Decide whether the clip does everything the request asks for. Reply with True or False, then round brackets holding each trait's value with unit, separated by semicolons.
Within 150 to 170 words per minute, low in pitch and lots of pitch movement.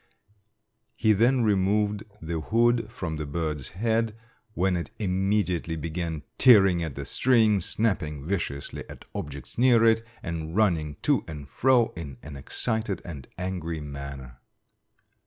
False (135 wpm; 90 Hz; 5.9 semitones)